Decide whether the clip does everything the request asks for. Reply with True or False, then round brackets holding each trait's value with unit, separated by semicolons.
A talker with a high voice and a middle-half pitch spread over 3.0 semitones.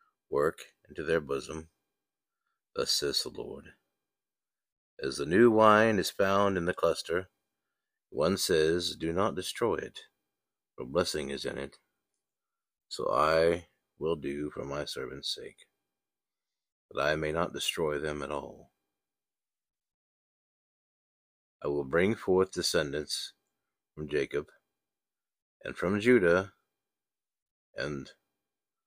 False (85 Hz; 4.7 semitones)